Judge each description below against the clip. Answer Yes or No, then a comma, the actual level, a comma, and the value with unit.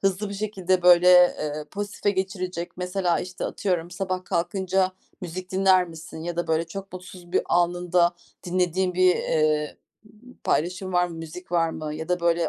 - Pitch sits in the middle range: Yes, medium, 180 Hz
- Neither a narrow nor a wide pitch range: No, narrow, 1.6 semitones